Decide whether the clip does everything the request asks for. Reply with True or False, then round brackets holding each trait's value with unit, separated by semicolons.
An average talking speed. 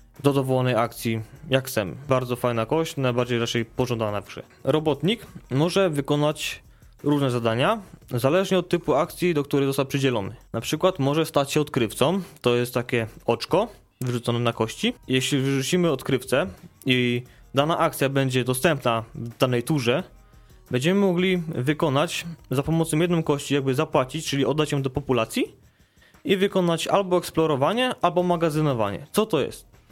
True (145 wpm)